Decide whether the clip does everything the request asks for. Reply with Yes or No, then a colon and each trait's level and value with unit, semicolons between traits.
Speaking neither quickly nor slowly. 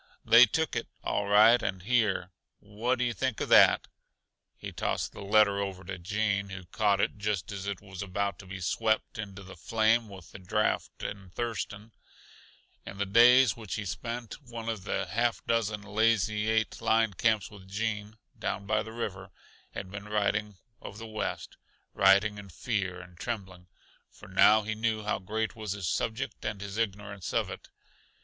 Yes: average, 180 wpm